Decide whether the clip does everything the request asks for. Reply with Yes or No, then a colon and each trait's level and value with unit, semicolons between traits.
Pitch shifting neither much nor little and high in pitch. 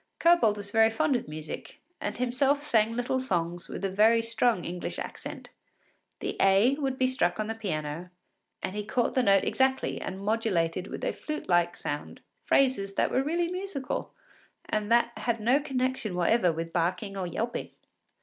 No: wide, 5.8 semitones; high, 225 Hz